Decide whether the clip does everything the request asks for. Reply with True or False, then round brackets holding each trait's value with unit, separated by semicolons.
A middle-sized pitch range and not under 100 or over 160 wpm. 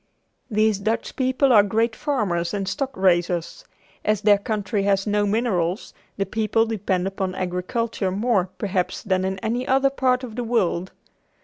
True (3.6 semitones; 155 wpm)